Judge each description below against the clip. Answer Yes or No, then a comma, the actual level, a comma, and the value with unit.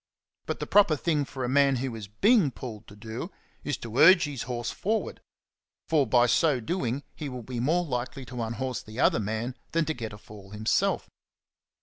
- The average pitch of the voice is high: No, low, 125 Hz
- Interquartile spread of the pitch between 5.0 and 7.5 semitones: No, average, 4.6 semitones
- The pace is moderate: No, fast, 215 wpm